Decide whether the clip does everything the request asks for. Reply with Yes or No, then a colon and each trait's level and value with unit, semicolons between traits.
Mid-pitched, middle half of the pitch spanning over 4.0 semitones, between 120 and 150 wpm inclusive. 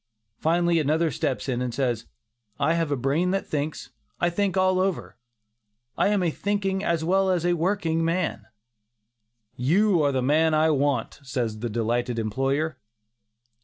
No: medium, 160 Hz; average, 5.0 semitones; average, 160 wpm